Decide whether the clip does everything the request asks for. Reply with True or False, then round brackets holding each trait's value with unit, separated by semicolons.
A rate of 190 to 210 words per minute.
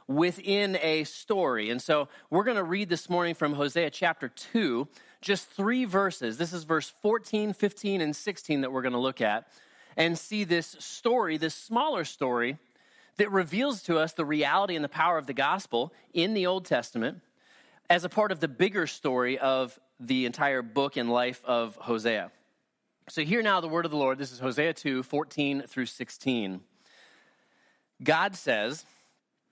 False (175 wpm)